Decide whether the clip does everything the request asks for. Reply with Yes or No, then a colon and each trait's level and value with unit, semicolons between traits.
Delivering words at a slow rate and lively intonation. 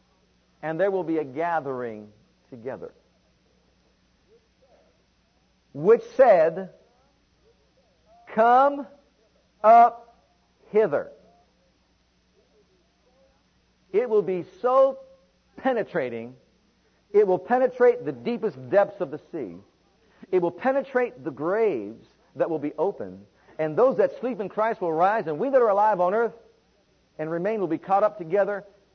Yes: slow, 120 wpm; wide, 7.0 semitones